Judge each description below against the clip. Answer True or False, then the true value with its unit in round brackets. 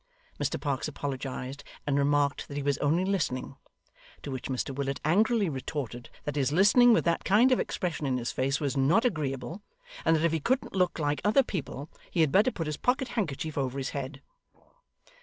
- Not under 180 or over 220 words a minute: True (195 wpm)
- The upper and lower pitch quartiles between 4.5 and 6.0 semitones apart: True (5.4 semitones)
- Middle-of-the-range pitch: True (145 Hz)